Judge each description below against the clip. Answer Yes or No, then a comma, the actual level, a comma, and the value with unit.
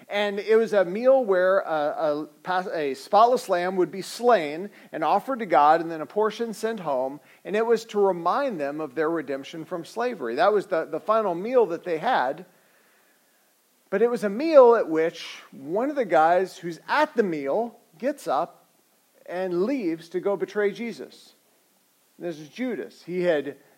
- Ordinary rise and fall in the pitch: No, wide, 5.9 semitones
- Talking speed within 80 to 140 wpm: No, average, 180 wpm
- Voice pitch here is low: No, high, 195 Hz